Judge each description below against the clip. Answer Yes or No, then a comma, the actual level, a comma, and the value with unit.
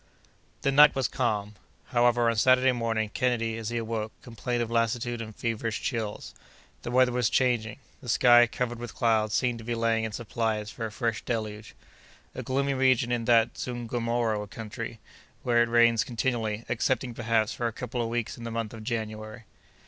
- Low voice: Yes, low, 115 Hz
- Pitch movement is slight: Yes, narrow, 1.5 semitones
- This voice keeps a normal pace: Yes, average, 180 wpm